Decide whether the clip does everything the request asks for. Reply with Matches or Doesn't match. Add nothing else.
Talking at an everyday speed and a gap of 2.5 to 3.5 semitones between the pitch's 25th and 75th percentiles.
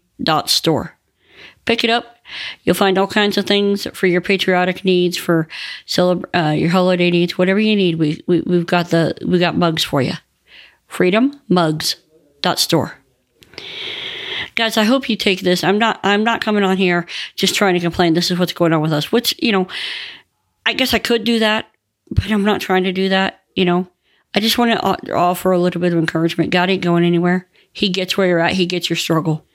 Doesn't match